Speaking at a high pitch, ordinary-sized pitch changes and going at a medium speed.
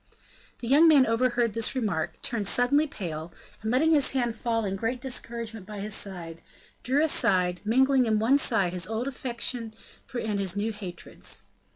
Yes: high, 225 Hz; average, 4.1 semitones; average, 170 wpm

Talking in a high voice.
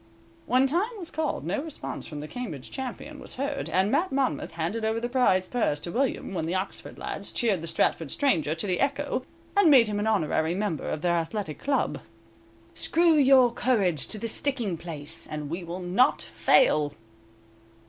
Yes: high, 210 Hz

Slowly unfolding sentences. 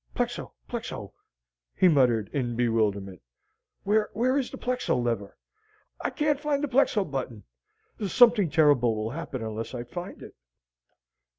Yes: slow, 130 wpm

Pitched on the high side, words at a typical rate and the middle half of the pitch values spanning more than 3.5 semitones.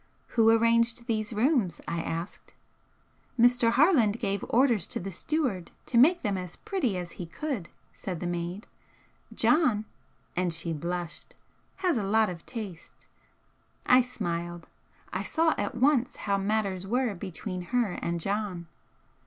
Yes: high, 210 Hz; average, 145 wpm; wide, 5.5 semitones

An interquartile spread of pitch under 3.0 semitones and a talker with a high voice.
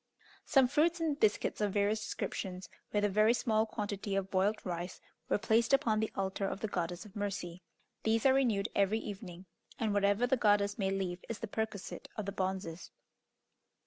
Yes: narrow, 2.5 semitones; high, 205 Hz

